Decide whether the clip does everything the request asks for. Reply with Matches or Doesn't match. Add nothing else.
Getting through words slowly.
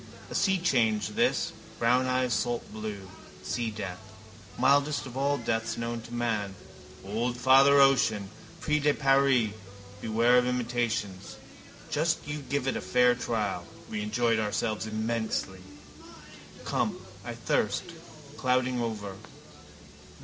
Matches